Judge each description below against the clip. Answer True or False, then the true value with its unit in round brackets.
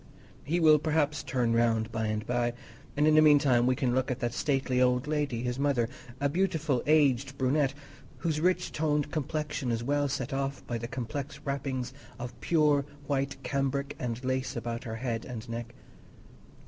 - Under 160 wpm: False (175 wpm)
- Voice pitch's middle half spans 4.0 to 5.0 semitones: False (3.4 semitones)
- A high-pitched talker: False (135 Hz)